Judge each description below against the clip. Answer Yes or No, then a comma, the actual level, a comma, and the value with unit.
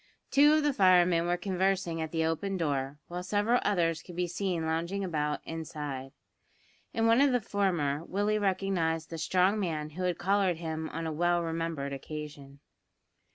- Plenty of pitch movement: No, average, 3.5 semitones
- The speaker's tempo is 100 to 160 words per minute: No, average, 170 wpm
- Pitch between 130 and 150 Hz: No, medium, 175 Hz